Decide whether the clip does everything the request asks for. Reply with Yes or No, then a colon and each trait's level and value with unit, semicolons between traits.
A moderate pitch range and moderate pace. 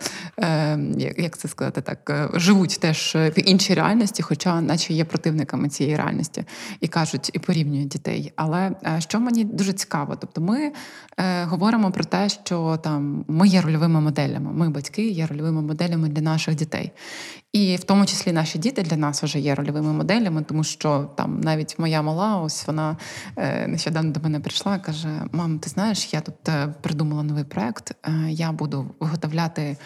No: average, 3.6 semitones; fast, 160 wpm